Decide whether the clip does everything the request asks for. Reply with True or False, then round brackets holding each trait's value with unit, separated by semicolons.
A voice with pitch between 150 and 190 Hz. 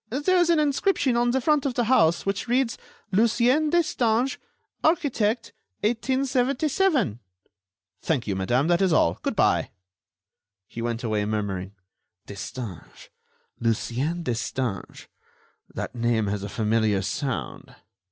True (185 Hz)